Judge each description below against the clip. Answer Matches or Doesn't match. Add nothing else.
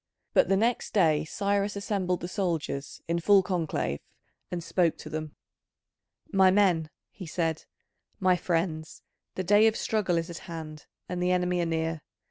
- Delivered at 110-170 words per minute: Matches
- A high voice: Doesn't match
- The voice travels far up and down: Doesn't match